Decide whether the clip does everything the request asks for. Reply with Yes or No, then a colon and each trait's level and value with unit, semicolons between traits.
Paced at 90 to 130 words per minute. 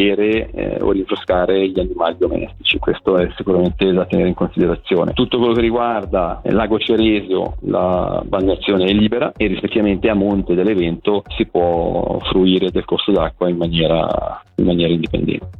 No: average, 150 wpm